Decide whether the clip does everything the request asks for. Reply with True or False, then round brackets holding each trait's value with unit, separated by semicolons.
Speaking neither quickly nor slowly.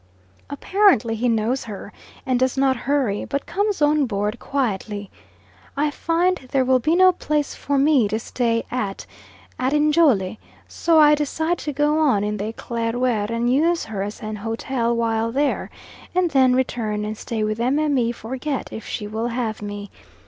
True (170 wpm)